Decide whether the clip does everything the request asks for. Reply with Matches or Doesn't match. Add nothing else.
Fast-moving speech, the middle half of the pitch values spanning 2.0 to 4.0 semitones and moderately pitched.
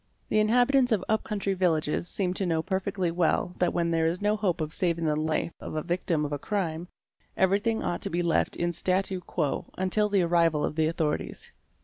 Matches